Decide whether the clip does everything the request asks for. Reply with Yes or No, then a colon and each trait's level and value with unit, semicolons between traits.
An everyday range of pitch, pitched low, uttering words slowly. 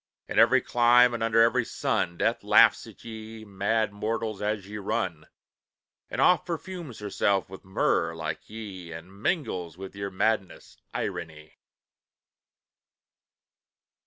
Yes: average, 3.2 semitones; low, 105 Hz; slow, 130 wpm